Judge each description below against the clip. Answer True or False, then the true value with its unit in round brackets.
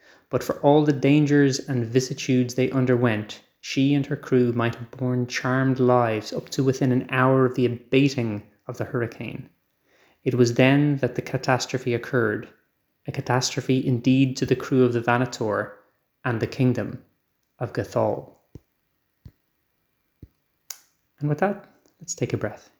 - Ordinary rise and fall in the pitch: False (1.8 semitones)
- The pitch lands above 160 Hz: False (130 Hz)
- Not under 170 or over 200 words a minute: False (150 wpm)